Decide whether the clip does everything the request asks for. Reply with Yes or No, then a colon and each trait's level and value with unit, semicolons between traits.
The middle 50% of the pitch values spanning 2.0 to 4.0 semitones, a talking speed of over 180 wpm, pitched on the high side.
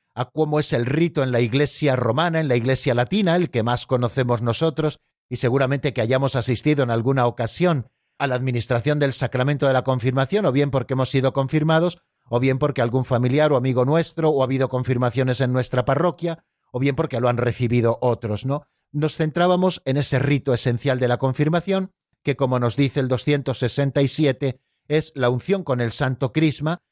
No: average, 3.3 semitones; fast, 190 wpm; low, 135 Hz